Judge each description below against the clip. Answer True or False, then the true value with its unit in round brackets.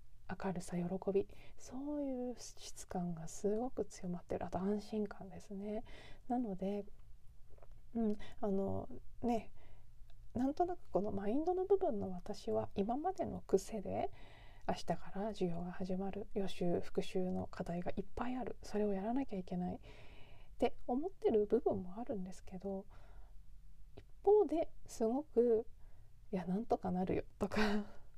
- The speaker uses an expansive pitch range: False (4.1 semitones)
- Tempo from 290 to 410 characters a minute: False (275 characters per minute)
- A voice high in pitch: True (205 Hz)